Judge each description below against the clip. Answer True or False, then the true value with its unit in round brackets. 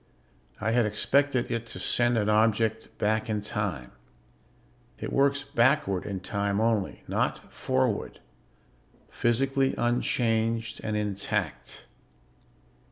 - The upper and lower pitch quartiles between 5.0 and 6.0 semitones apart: False (2.5 semitones)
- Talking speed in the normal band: False (105 wpm)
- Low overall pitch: True (110 Hz)